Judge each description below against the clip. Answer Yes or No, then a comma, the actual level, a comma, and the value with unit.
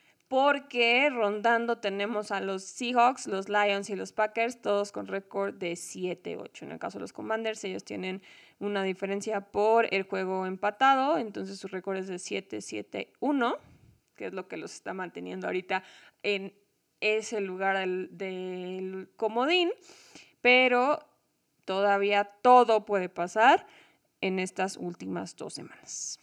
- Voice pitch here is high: Yes, high, 200 Hz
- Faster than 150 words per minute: No, average, 135 wpm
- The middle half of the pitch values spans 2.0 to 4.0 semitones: Yes, average, 3.5 semitones